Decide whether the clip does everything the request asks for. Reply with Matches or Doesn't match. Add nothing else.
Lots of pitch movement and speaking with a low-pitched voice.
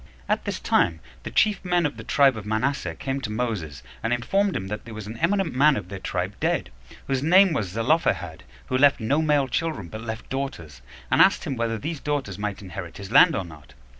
Matches